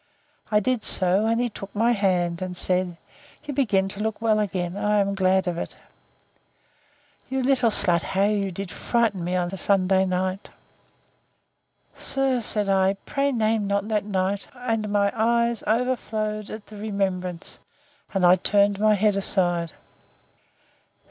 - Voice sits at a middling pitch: No, high, 200 Hz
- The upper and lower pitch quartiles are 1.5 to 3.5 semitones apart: Yes, average, 2.8 semitones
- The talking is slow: No, average, 150 wpm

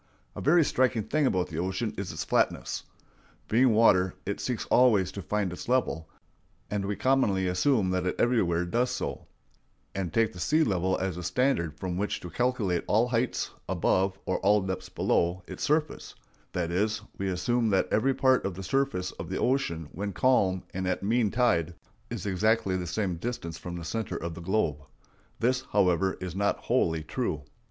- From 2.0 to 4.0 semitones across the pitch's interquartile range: No, average, 5.0 semitones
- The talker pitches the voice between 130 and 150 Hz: No, very low, 95 Hz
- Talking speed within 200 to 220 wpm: No, average, 180 wpm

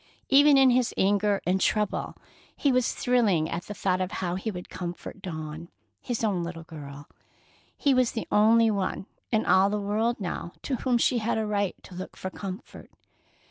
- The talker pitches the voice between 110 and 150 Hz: No, high, 200 Hz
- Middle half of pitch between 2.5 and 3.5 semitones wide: No, average, 4.4 semitones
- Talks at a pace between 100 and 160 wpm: No, average, 185 wpm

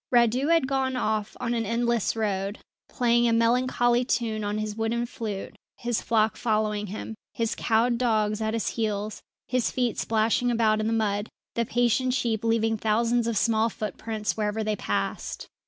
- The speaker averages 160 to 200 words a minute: Yes, average, 170 wpm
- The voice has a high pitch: Yes, high, 225 Hz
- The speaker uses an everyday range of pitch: No, narrow, 1.8 semitones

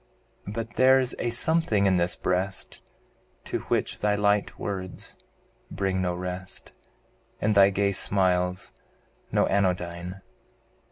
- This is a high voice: No, very low, 95 Hz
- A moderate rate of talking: No, slow, 115 wpm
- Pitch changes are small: Yes, narrow, 2.2 semitones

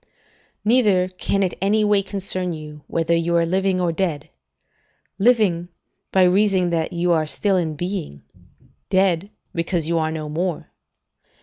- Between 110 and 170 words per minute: Yes, average, 145 wpm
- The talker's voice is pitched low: No, medium, 180 Hz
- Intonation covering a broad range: No, average, 2.7 semitones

